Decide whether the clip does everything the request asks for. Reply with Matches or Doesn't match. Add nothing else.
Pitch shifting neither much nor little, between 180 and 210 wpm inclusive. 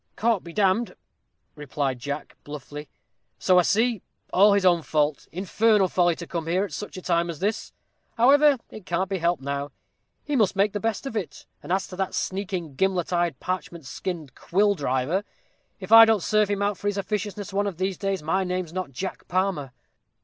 Matches